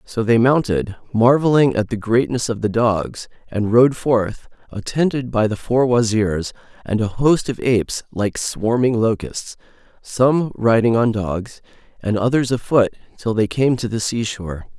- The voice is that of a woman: No, male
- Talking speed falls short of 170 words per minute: Yes, average, 160 wpm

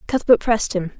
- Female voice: Yes, female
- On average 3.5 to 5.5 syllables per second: No, 6.1 syllables/s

